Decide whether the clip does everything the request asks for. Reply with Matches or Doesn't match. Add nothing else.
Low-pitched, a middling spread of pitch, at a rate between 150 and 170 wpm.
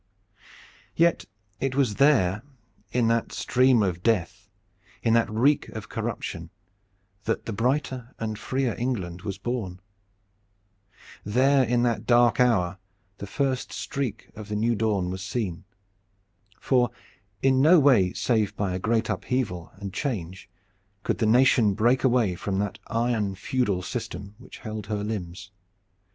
Doesn't match